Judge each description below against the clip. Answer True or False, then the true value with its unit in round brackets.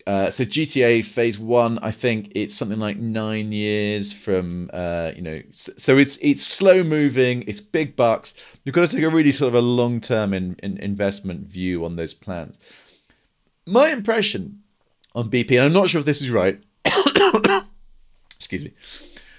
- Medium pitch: False (115 Hz)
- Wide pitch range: True (6.1 semitones)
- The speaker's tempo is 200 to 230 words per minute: False (175 wpm)